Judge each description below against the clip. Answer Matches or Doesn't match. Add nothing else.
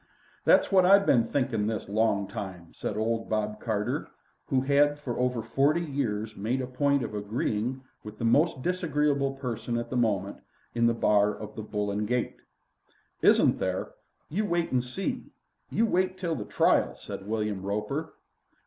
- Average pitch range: Matches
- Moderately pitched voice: Doesn't match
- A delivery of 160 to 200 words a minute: Matches